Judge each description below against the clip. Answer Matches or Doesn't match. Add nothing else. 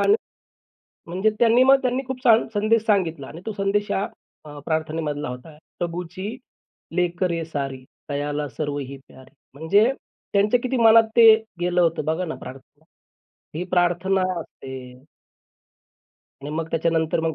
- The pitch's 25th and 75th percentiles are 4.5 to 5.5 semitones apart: Matches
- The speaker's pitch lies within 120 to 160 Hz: Doesn't match